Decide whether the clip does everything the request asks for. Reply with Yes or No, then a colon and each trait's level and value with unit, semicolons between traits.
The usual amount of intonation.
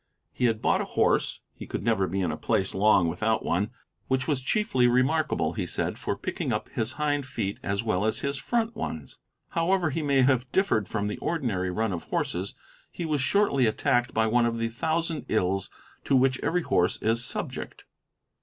No: wide, 5.8 semitones